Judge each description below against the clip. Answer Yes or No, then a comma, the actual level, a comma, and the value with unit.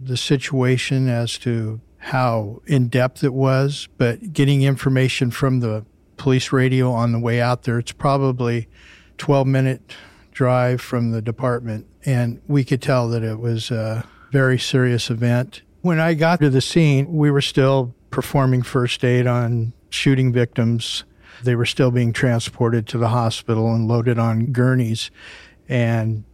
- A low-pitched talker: Yes, low, 125 Hz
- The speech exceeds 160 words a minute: No, average, 155 wpm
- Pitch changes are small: Yes, narrow, 2.3 semitones